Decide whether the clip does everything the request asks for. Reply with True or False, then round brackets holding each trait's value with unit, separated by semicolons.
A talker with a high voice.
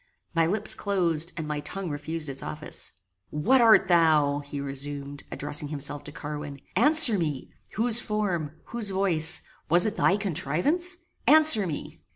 False (165 Hz)